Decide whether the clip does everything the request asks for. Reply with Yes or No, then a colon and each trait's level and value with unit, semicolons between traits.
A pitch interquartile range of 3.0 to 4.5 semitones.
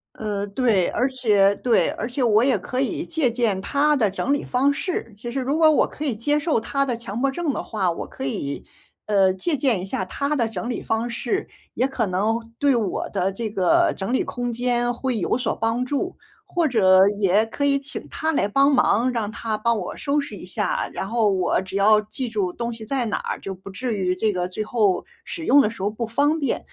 No: average, 4.9 semitones